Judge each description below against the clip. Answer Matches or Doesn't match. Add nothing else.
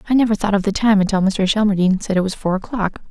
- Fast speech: Matches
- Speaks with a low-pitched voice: Doesn't match